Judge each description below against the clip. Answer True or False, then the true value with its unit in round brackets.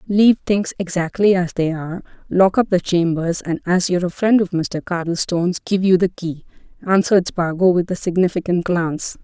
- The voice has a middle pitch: True (180 Hz)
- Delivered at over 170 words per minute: True (180 wpm)